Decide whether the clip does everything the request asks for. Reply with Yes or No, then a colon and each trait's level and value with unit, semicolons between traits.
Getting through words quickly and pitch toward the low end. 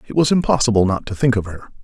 Yes: fast, 260 wpm; low, 120 Hz